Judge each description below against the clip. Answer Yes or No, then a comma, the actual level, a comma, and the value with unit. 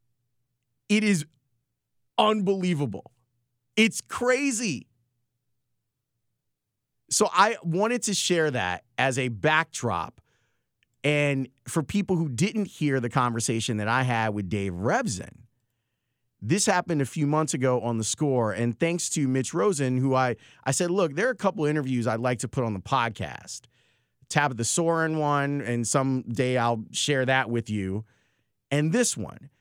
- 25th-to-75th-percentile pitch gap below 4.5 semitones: No, average, 5.0 semitones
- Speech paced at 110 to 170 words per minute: Yes, average, 150 wpm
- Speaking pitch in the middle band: No, low, 130 Hz